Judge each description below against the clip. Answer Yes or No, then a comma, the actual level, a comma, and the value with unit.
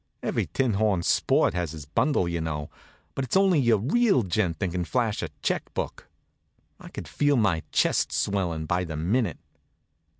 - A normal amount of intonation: No, wide, 6.8 semitones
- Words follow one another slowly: No, average, 170 wpm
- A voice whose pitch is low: Yes, very low, 95 Hz